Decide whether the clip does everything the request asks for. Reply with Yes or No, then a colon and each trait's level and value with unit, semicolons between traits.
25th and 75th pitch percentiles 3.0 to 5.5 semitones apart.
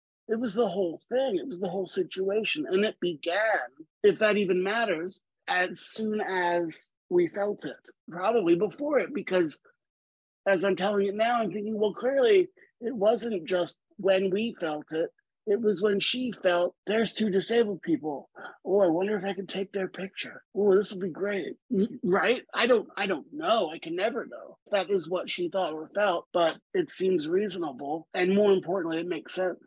Yes: average, 3.6 semitones